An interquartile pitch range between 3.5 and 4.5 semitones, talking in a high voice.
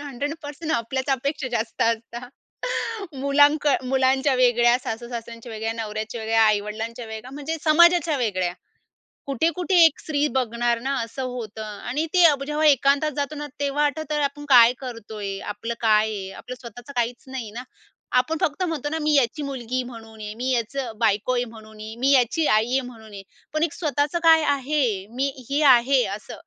Yes: average, 4.1 semitones; very high, 255 Hz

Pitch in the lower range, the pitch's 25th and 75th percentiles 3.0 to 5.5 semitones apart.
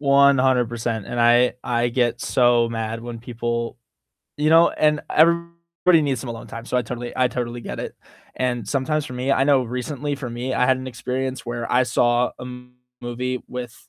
No: low, 125 Hz; narrow, 2.5 semitones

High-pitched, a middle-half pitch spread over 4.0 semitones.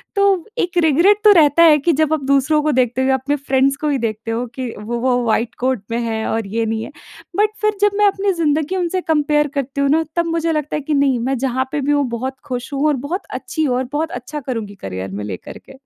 Yes: very high, 280 Hz; average, 4.4 semitones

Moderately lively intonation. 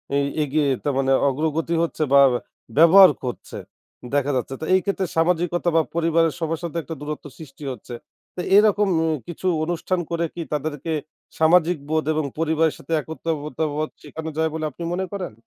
No: narrow, 2.0 semitones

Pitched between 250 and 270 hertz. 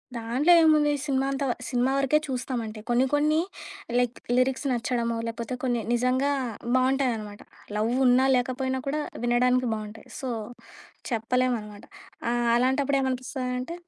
Yes: very high, 255 Hz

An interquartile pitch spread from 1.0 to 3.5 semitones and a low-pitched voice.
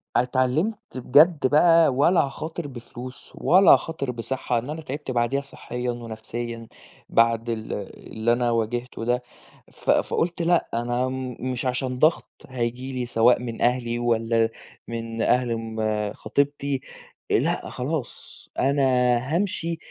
Yes: average, 3.2 semitones; low, 125 Hz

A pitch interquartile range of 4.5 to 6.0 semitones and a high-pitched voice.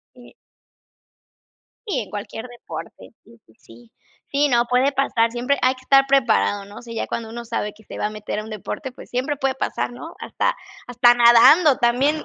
No: average, 3.2 semitones; high, 240 Hz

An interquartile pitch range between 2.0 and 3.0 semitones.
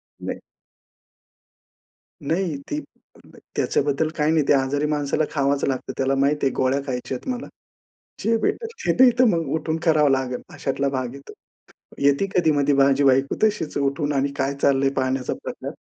Yes: average, 2.7 semitones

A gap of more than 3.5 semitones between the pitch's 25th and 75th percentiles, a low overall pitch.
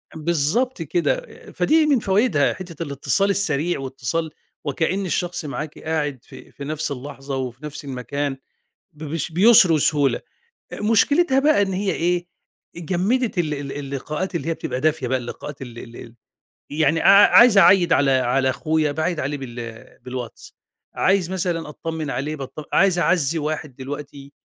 No: average, 4.4 semitones; medium, 155 Hz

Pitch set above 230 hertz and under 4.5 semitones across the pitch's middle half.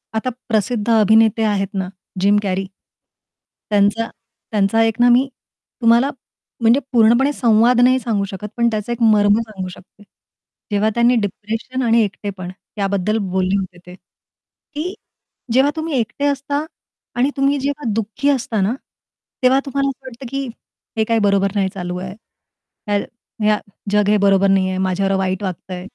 No: high, 220 Hz; average, 3.7 semitones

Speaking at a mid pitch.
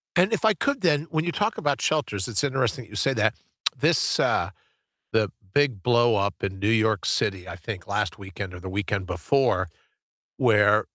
No: low, 110 Hz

